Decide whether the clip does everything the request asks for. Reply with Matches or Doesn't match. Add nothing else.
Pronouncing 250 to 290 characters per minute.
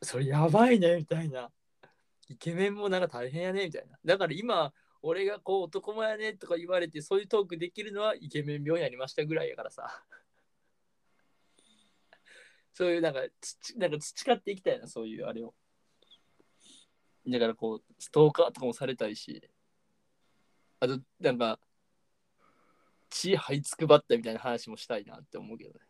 Doesn't match